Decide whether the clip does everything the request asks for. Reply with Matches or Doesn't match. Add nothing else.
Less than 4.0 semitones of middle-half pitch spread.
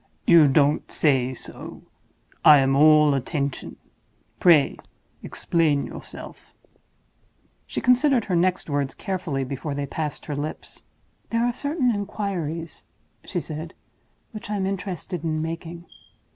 Doesn't match